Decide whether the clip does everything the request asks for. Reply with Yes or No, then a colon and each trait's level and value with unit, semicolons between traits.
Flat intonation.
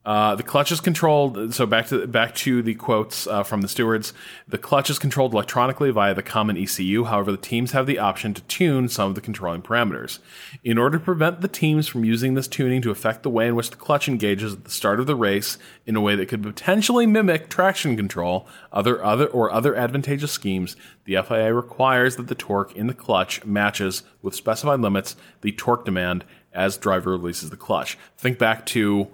No: average, 4.6 semitones